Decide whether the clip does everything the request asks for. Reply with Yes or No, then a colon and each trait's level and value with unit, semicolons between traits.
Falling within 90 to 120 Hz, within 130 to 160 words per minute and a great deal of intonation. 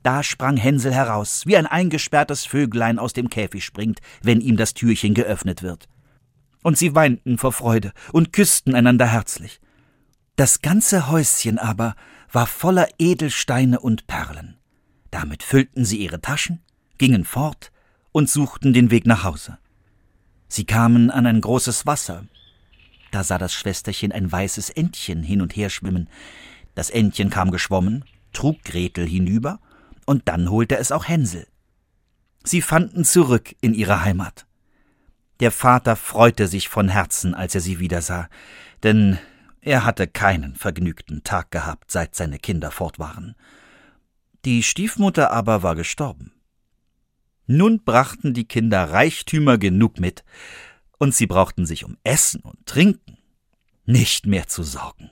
Yes: low, 115 Hz; average, 145 wpm; wide, 6.1 semitones